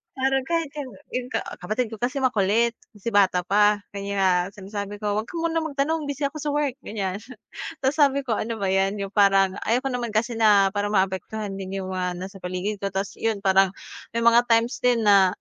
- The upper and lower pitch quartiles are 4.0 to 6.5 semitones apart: Yes, average, 4.3 semitones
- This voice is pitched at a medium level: No, high, 210 Hz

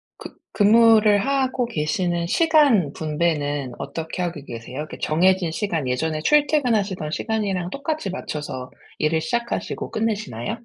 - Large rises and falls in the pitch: Yes, wide, 6.9 semitones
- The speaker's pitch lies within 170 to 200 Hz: Yes, medium, 185 Hz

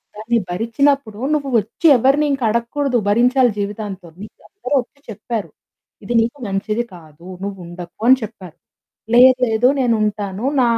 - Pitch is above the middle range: Yes, high, 230 Hz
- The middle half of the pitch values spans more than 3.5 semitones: Yes, average, 4.0 semitones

